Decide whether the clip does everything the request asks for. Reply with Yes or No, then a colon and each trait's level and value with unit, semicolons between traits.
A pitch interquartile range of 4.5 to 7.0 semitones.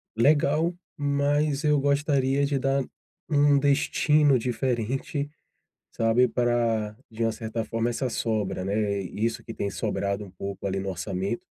Yes: average, 4.8 semitones